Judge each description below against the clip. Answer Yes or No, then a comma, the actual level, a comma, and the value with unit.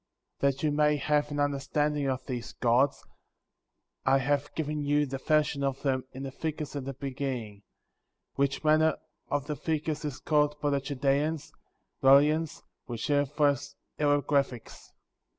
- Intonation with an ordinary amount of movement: No, narrow, 1.6 semitones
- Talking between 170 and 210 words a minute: No, average, 150 wpm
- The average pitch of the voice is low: No, medium, 145 Hz